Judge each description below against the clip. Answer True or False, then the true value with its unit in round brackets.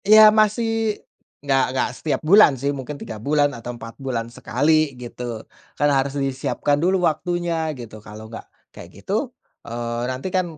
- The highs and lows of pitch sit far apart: True (6.2 semitones)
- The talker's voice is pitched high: False (140 Hz)